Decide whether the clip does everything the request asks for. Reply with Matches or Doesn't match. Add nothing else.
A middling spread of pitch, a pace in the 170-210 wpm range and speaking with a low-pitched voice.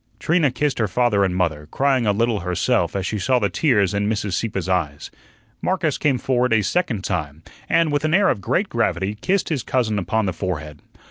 Doesn't match